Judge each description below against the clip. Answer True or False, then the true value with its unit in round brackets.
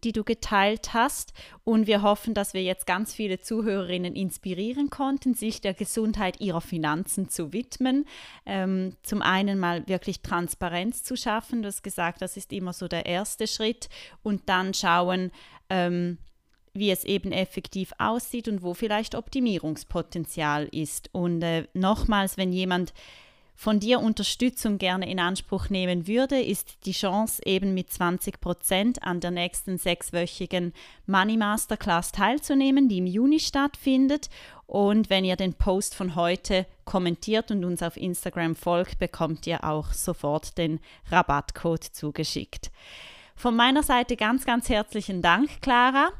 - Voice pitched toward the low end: False (190 Hz)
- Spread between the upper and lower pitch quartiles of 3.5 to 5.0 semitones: True (3.8 semitones)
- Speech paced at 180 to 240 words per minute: False (145 wpm)